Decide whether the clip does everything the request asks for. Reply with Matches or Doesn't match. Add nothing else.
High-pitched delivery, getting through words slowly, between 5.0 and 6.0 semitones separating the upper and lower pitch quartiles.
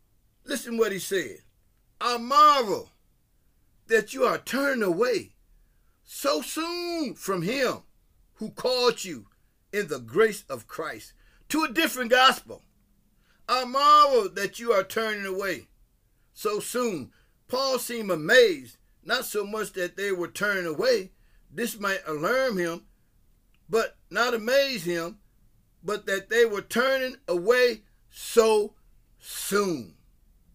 Matches